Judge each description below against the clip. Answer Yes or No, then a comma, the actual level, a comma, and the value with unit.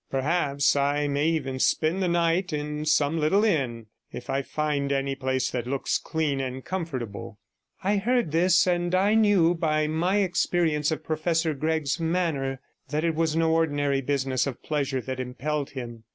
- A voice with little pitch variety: No, average, 3.4 semitones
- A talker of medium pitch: Yes, medium, 150 Hz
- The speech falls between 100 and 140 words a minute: No, average, 165 wpm